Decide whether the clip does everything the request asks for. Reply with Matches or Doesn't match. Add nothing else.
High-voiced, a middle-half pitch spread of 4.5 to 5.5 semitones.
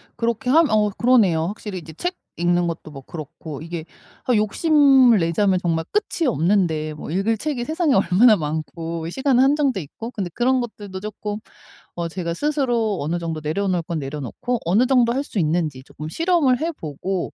Doesn't match